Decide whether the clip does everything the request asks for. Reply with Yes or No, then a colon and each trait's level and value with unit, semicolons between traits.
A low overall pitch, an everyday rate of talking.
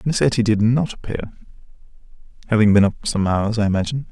Yes: low, 110 Hz; average, 175 wpm